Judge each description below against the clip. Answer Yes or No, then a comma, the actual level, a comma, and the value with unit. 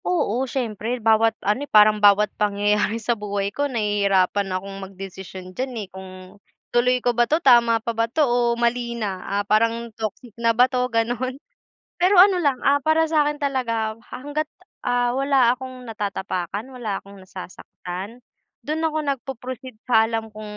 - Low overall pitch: No, high, 230 Hz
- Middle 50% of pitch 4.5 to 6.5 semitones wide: No, average, 3.8 semitones